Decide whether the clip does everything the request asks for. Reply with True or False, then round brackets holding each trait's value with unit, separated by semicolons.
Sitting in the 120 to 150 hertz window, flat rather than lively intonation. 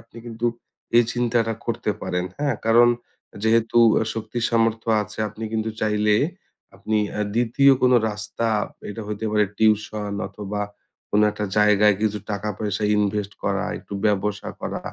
False (110 Hz; 1.5 semitones)